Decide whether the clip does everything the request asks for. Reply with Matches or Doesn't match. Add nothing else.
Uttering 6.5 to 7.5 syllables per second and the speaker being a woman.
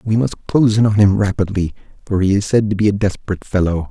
Doesn't match